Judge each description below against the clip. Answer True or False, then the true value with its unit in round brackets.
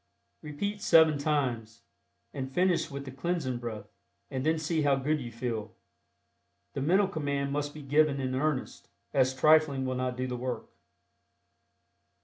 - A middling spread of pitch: True (3.2 semitones)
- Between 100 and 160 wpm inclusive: True (150 wpm)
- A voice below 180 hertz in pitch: True (140 Hz)